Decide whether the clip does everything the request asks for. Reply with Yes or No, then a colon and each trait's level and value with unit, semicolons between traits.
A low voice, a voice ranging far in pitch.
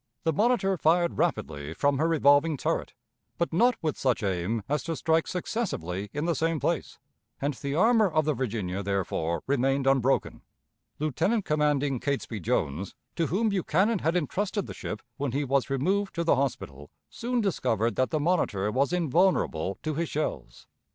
No: medium, 145 Hz; wide, 6.3 semitones